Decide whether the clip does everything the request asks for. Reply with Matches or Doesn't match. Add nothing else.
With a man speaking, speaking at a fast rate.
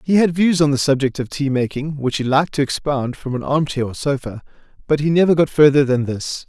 Matches